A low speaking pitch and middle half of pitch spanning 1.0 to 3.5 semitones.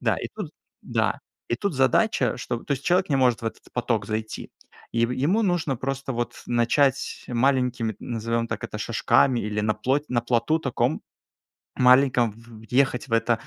Yes: low, 125 Hz; average, 2.9 semitones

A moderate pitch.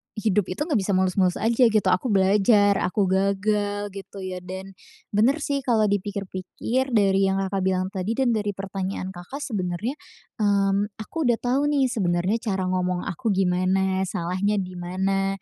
No: high, 195 Hz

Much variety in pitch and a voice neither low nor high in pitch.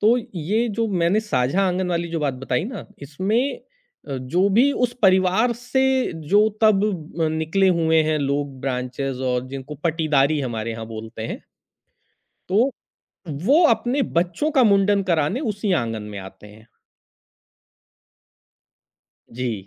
Yes: wide, 7.7 semitones; medium, 170 Hz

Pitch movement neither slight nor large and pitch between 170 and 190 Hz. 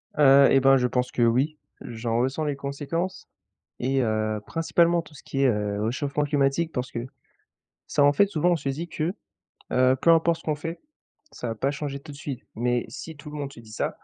No: average, 3.6 semitones; medium, 140 Hz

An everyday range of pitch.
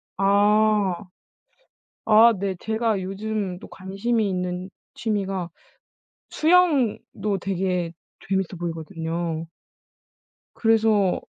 Yes: average, 3.1 semitones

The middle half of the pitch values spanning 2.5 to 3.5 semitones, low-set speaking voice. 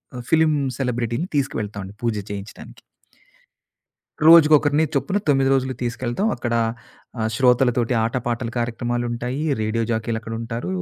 Yes: average, 2.8 semitones; low, 120 Hz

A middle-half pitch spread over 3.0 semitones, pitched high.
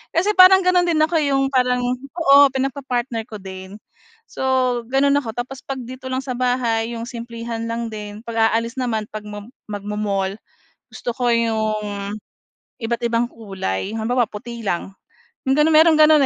Yes: average, 3.6 semitones; high, 235 Hz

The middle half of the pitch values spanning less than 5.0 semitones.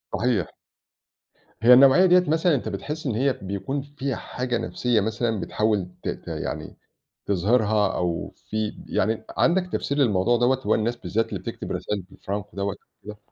Yes: average, 4.5 semitones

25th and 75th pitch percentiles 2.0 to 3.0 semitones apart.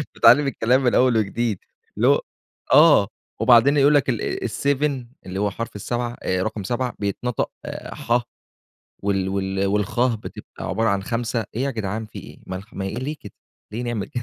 No: average, 3.7 semitones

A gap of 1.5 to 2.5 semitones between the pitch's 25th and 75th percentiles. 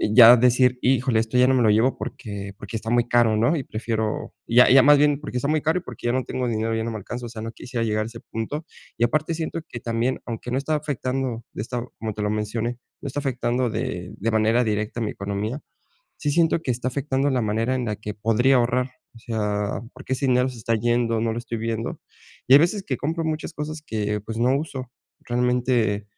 No: average, 2.9 semitones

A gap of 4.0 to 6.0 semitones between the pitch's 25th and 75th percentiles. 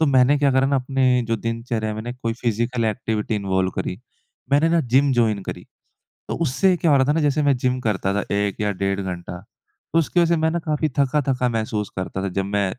Yes: average, 5.1 semitones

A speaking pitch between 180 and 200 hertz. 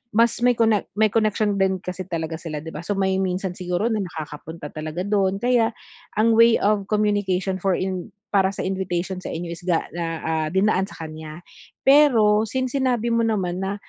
Yes: high, 190 Hz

